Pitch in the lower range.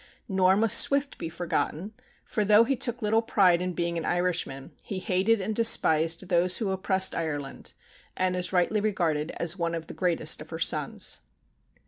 No: medium, 185 Hz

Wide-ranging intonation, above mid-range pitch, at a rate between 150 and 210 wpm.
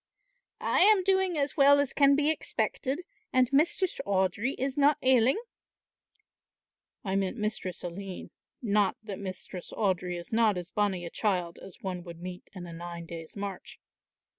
Yes: wide, 7.3 semitones; high, 205 Hz; average, 160 wpm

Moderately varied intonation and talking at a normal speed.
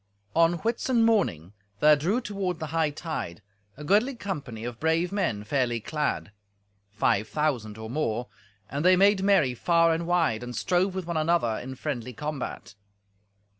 No: wide, 6.8 semitones; average, 155 wpm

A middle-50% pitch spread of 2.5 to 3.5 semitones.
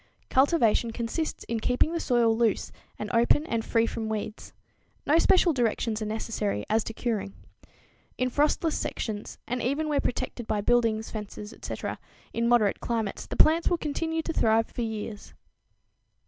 No: average, 4.3 semitones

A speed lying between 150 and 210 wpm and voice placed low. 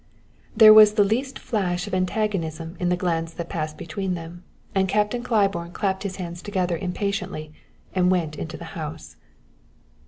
No: average, 160 wpm; medium, 185 Hz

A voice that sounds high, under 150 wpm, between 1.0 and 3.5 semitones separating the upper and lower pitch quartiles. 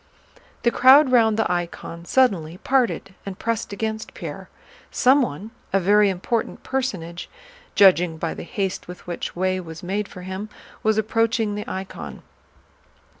No: high, 200 Hz; average, 140 wpm; average, 4.1 semitones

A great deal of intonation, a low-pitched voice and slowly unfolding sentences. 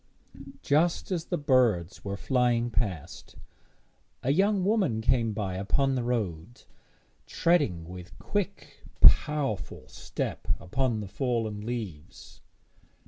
Yes: wide, 6.3 semitones; low, 120 Hz; slow, 110 wpm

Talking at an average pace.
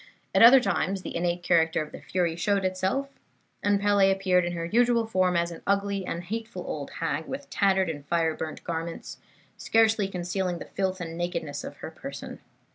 Yes: average, 190 wpm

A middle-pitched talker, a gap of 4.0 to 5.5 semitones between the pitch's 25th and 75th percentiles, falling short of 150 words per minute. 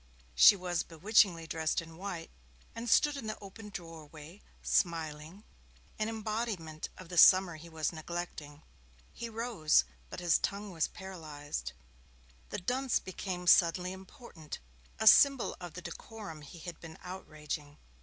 Yes: medium, 175 Hz; average, 4.5 semitones; average, 140 wpm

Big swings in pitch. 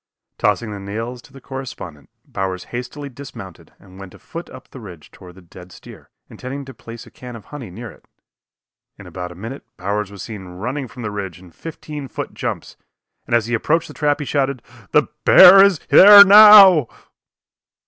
Yes: wide, 6.6 semitones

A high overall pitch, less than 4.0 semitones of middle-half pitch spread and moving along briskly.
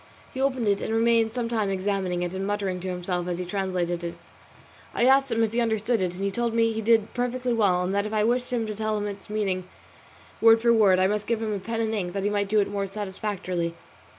Yes: high, 210 Hz; average, 3.3 semitones; fast, 255 wpm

